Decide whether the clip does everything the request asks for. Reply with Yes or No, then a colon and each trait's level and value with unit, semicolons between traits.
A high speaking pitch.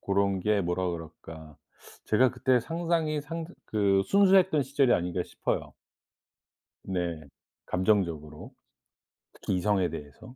No: low, 100 Hz